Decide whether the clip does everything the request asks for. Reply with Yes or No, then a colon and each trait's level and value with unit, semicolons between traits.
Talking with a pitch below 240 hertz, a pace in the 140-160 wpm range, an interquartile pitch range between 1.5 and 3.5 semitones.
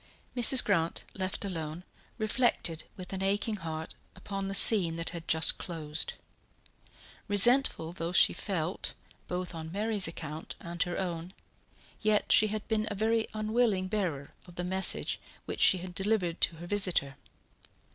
No: medium, 185 Hz; average, 150 wpm; average, 3.9 semitones